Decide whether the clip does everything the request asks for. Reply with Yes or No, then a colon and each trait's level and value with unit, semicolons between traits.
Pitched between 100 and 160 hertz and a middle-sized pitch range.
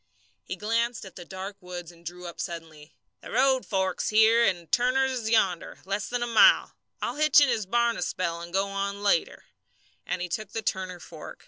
No: high, 195 Hz; average, 4.8 semitones